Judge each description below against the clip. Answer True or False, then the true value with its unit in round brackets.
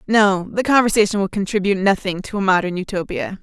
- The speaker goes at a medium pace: True (175 wpm)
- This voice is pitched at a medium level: False (200 Hz)